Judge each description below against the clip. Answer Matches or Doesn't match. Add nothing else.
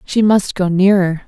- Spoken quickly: Doesn't match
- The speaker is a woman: Matches